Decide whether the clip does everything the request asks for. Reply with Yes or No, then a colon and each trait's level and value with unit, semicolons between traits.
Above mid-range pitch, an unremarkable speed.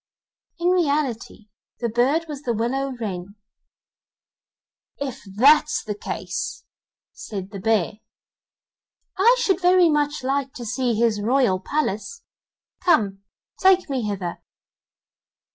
No: very high, 255 Hz; slow, 110 wpm